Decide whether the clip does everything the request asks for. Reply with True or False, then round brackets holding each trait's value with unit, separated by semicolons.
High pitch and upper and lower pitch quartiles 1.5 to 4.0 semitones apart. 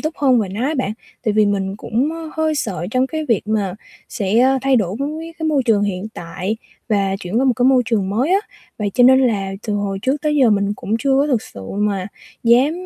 False (230 Hz; 5.0 semitones)